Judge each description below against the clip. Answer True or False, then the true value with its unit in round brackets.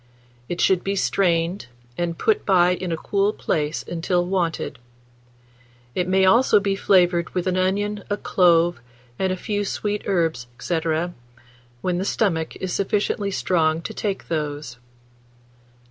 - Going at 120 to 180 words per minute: True (145 wpm)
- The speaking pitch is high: False (180 Hz)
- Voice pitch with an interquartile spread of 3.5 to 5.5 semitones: False (2.8 semitones)